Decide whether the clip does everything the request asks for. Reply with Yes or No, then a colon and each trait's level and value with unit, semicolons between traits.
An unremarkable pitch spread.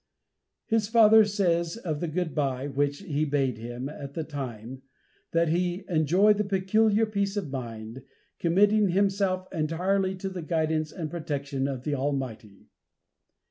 No: wide, 5.7 semitones